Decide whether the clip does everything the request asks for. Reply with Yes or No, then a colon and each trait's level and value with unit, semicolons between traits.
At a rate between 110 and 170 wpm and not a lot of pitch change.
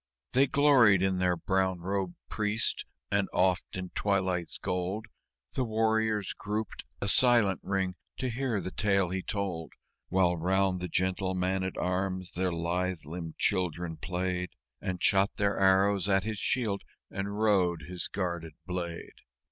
Yes: average, 150 wpm; narrow, 2.0 semitones